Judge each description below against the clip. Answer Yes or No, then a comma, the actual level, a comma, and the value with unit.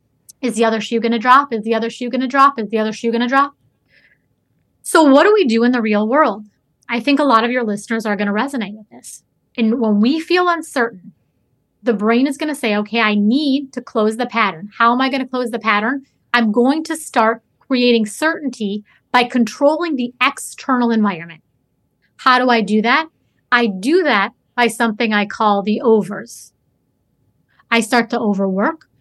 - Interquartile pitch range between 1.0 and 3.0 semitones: No, average, 3.4 semitones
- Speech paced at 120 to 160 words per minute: No, fast, 205 wpm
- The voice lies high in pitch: Yes, high, 235 Hz